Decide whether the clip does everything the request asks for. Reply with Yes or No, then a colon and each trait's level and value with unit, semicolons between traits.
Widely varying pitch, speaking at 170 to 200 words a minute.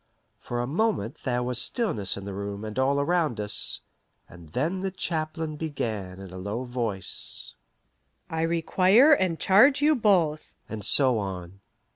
No: wide, 9.0 semitones; average, 160 wpm